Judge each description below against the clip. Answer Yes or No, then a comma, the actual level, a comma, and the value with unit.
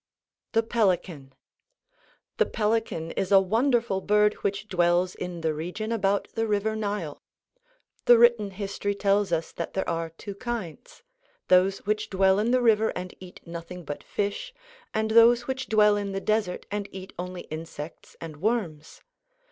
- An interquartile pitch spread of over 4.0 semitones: No, average, 3.5 semitones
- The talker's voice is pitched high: Yes, high, 200 Hz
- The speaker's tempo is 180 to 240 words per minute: No, average, 155 wpm